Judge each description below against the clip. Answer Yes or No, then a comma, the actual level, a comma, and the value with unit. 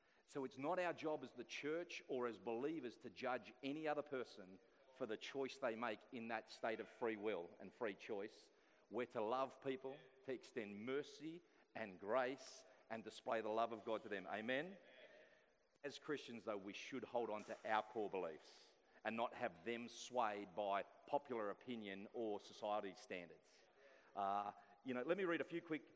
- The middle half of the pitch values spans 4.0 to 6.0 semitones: Yes, average, 4.9 semitones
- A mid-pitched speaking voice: No, low, 120 Hz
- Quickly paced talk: No, average, 185 wpm